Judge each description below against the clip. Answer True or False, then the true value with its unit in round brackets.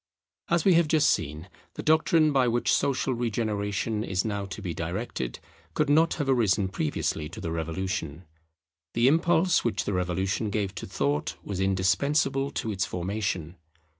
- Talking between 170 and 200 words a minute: False (160 wpm)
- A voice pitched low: True (105 Hz)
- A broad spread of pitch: True (6.9 semitones)